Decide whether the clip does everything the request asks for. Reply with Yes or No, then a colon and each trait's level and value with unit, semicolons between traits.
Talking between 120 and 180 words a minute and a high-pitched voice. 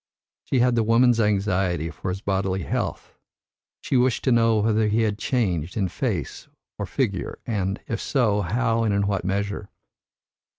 No: average, 165 wpm; low, 105 Hz